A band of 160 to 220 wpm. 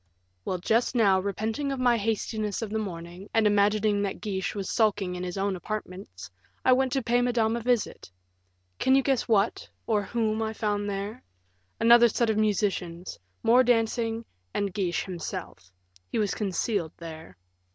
Yes: average, 165 wpm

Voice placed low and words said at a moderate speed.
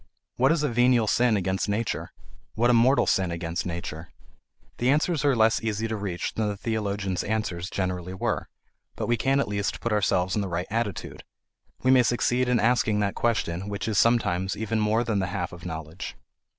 Yes: low, 105 Hz; average, 195 wpm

